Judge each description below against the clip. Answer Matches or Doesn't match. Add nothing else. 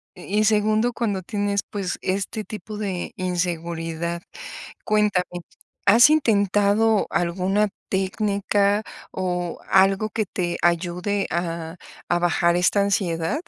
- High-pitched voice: Matches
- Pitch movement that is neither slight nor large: Matches